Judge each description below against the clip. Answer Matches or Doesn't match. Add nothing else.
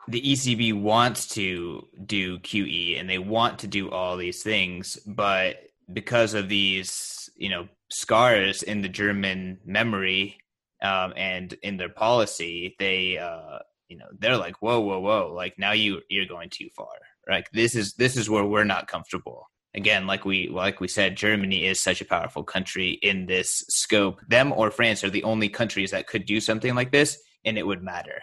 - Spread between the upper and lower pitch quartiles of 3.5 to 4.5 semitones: Doesn't match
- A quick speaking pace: Doesn't match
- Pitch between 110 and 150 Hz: Doesn't match